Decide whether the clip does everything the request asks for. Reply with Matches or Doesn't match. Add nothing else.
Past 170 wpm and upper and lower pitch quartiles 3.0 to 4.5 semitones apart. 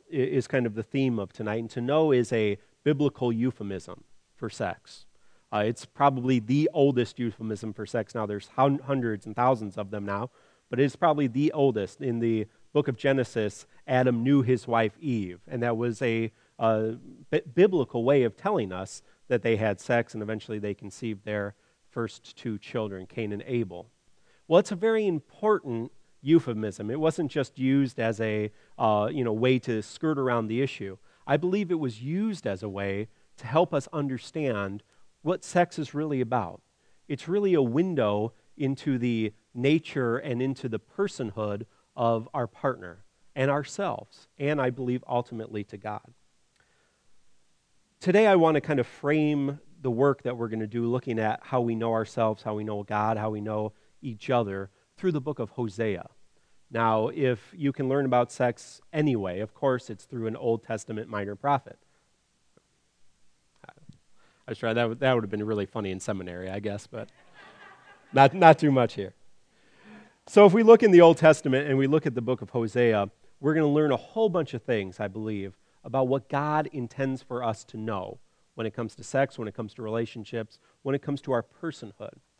Matches